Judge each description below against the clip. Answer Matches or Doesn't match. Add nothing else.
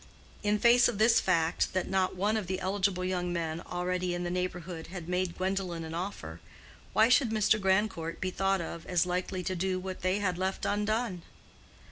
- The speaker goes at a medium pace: Matches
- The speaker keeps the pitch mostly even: Matches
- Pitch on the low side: Doesn't match